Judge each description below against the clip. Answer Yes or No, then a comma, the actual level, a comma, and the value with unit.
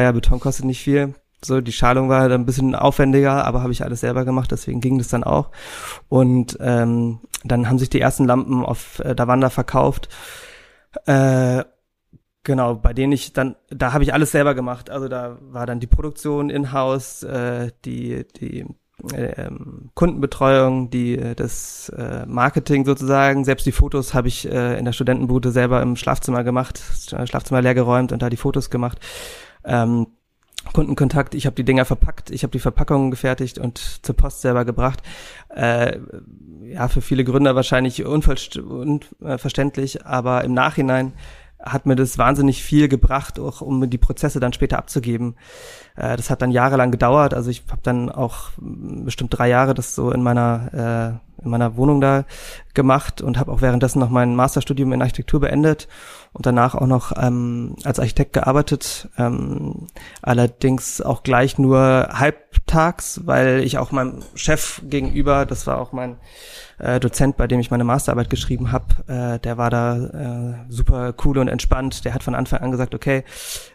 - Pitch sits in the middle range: No, low, 130 Hz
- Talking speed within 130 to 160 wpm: No, average, 170 wpm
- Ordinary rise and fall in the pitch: No, narrow, 2.0 semitones